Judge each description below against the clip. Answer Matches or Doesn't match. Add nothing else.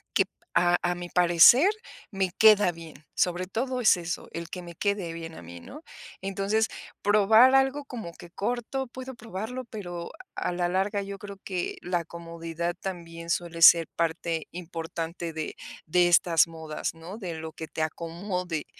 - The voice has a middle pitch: Matches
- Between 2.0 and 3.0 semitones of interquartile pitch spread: Doesn't match